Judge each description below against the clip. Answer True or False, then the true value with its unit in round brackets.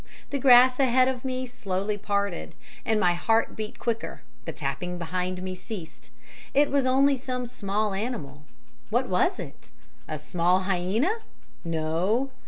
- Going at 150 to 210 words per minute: False (140 wpm)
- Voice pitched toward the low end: False (210 Hz)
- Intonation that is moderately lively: False (5.8 semitones)